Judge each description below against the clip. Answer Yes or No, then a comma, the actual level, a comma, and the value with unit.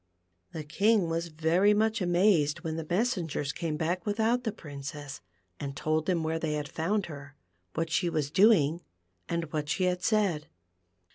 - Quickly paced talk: No, average, 170 wpm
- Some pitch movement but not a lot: Yes, average, 4.2 semitones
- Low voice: No, medium, 165 Hz